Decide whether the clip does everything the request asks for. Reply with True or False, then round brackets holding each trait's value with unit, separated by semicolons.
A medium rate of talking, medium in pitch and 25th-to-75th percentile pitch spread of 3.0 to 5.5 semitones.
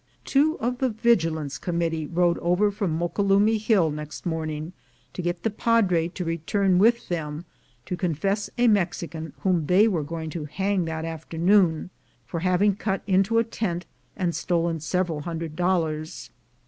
True (155 wpm; 175 Hz; 3.7 semitones)